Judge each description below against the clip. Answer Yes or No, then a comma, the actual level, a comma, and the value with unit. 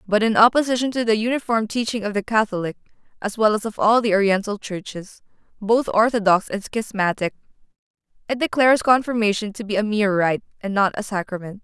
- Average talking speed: Yes, average, 175 wpm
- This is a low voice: No, high, 215 Hz